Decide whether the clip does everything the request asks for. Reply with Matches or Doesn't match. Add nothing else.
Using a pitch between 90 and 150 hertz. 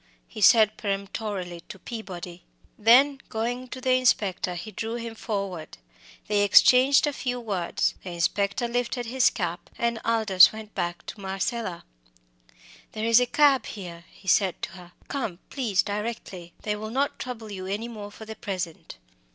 Doesn't match